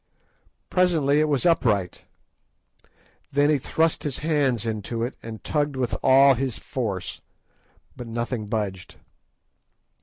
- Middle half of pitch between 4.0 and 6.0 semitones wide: Yes, average, 4.4 semitones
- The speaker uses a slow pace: Yes, slow, 120 wpm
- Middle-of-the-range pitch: No, low, 130 Hz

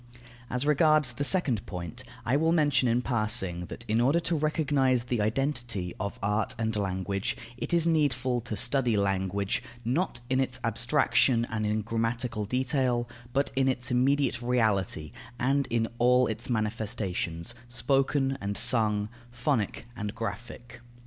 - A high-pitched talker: No, low, 120 Hz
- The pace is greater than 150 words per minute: No, average, 145 wpm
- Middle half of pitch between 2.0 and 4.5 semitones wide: Yes, average, 3.9 semitones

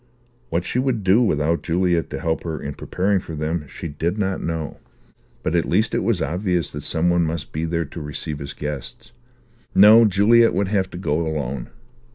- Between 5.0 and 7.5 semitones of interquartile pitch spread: No, average, 4.1 semitones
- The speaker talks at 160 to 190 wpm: No, average, 200 wpm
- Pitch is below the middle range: Yes, very low, 85 Hz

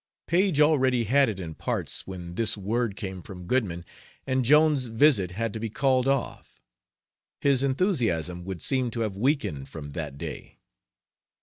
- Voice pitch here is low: Yes, low, 115 Hz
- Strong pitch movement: Yes, wide, 6.6 semitones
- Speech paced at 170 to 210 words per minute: No, average, 160 wpm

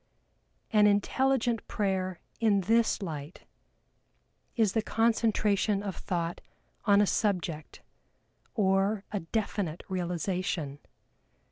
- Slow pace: Yes, slow, 95 wpm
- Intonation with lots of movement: No, average, 3.3 semitones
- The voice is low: No, high, 200 Hz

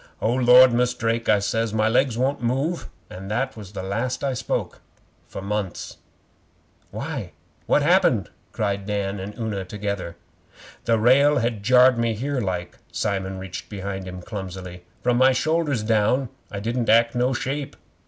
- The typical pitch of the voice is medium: No, low, 115 Hz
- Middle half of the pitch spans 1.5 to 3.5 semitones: No, average, 4.1 semitones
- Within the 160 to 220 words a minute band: Yes, average, 165 wpm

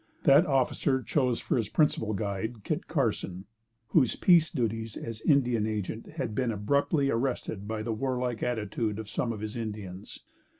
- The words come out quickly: No, average, 160 wpm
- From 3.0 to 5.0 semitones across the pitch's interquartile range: Yes, average, 3.7 semitones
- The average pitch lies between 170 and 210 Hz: No, low, 115 Hz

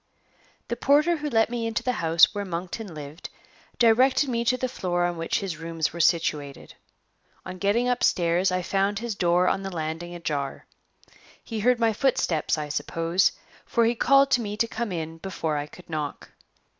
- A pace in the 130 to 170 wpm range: No, average, 180 wpm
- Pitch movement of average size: No, wide, 5.9 semitones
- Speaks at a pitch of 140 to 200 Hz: Yes, high, 190 Hz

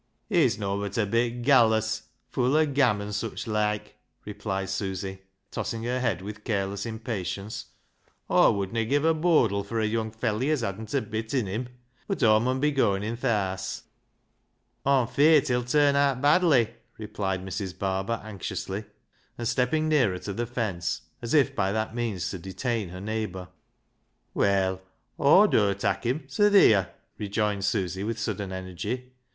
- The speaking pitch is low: Yes, low, 110 Hz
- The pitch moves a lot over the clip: No, average, 4.2 semitones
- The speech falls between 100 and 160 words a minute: No, average, 170 wpm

